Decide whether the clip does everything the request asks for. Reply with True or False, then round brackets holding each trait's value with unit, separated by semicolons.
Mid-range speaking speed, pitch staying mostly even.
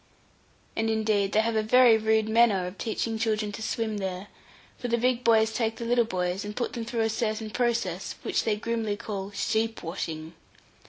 True (195 wpm; 2.0 semitones)